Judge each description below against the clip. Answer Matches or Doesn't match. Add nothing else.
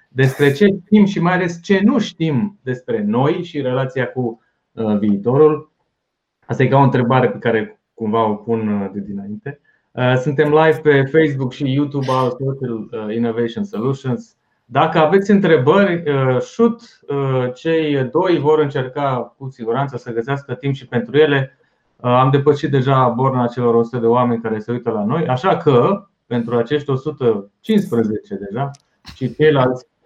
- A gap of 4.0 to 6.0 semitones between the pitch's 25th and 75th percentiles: Matches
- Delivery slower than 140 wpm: Doesn't match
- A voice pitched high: Doesn't match